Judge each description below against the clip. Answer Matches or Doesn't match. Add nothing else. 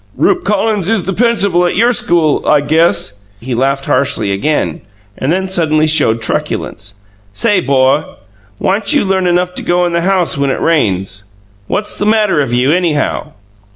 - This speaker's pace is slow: Doesn't match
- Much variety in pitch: Matches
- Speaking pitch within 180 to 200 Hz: Doesn't match